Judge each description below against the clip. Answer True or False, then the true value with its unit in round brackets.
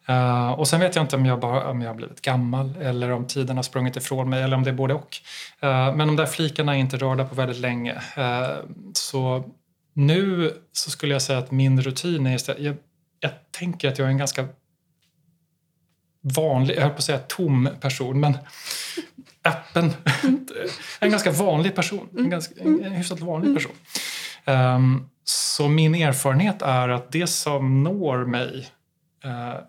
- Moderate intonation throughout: True (3.8 semitones)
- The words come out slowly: False (175 wpm)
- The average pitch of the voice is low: False (145 Hz)